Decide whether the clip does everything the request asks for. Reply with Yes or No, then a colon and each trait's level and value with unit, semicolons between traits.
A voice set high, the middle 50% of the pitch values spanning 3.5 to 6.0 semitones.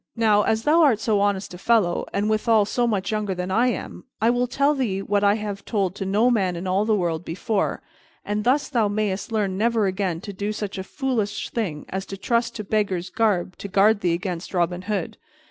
No: high, 205 Hz; average, 2.9 semitones